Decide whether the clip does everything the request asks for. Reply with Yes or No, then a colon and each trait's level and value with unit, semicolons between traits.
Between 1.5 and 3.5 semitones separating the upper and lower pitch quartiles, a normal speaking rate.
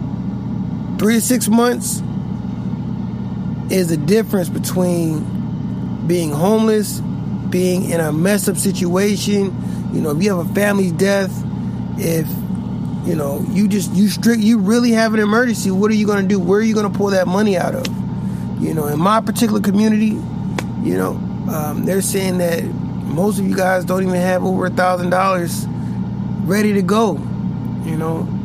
Yes: average, 2.7 semitones; average, 165 wpm